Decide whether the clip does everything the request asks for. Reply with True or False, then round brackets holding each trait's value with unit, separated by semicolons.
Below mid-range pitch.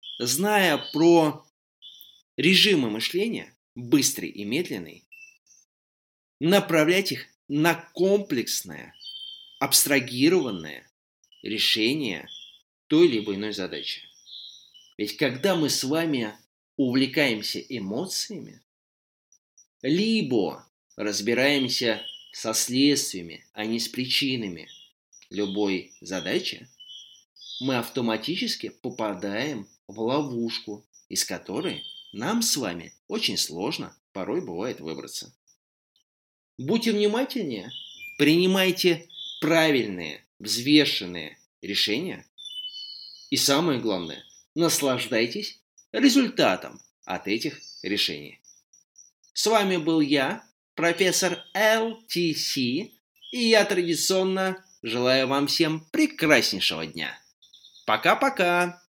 False (155 Hz)